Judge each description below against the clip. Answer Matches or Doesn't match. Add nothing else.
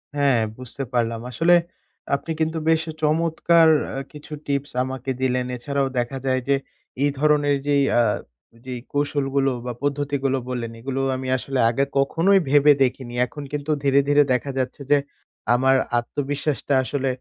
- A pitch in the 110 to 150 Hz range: Matches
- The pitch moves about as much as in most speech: Doesn't match